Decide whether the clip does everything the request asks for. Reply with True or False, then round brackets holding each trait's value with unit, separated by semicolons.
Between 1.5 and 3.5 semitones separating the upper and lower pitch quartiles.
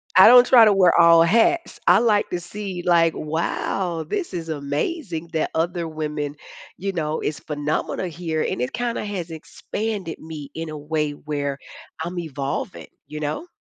False (4.0 semitones)